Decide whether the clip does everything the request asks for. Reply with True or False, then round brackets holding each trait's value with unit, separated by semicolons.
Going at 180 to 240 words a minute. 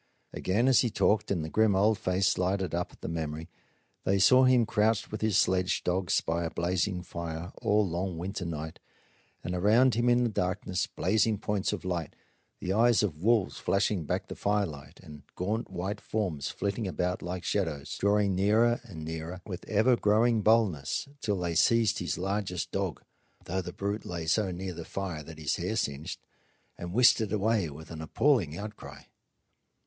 True (185 wpm)